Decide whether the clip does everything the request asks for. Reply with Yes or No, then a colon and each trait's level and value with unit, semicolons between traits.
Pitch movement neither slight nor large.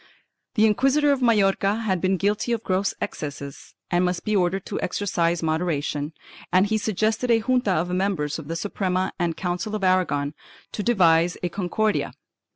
Yes: average, 3.8 semitones